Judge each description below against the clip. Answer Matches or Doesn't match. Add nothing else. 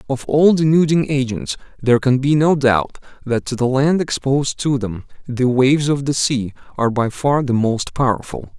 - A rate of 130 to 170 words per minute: Doesn't match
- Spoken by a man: Matches